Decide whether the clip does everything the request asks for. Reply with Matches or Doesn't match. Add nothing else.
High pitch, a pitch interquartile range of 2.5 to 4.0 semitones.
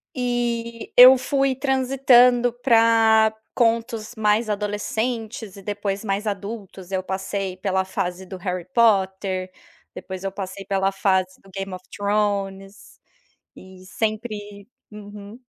Matches